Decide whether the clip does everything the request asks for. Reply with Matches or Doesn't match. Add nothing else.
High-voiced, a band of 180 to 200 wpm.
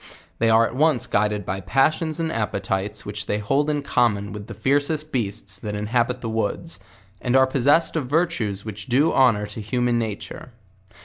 Doesn't match